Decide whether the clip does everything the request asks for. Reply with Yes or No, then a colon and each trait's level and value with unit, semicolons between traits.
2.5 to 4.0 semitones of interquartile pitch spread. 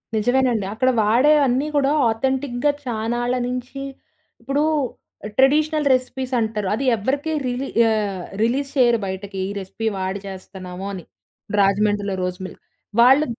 No: average, 4.7 semitones